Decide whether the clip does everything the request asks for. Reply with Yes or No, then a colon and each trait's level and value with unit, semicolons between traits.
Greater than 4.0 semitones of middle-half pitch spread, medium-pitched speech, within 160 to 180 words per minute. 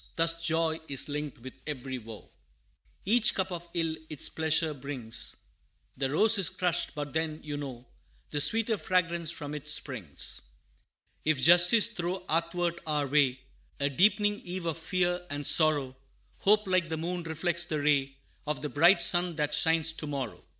No: average, 3.3 semitones; medium, 160 Hz; average, 165 wpm